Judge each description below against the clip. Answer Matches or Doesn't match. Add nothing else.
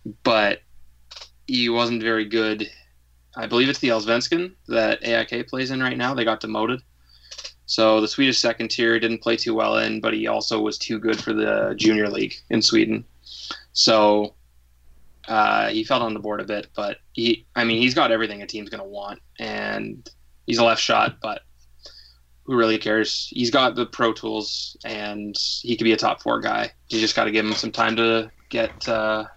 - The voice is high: Doesn't match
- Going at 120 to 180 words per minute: Doesn't match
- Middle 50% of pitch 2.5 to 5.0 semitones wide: Doesn't match